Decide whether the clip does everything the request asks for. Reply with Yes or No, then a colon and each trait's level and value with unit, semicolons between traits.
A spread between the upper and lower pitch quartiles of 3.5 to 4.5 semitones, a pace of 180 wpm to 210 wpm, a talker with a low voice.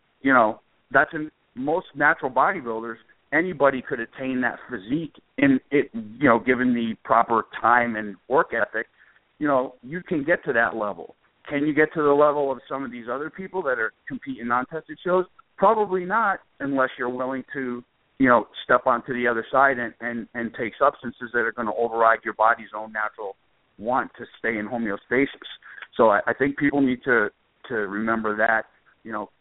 Yes: average, 4.2 semitones; average, 190 wpm; low, 125 Hz